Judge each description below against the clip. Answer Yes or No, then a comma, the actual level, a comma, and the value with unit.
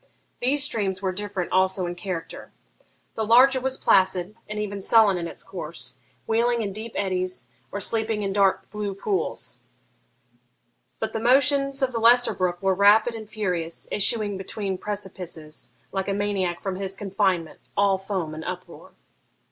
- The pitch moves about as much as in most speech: Yes, average, 3.0 semitones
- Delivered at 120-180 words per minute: Yes, average, 160 wpm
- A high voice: Yes, high, 200 Hz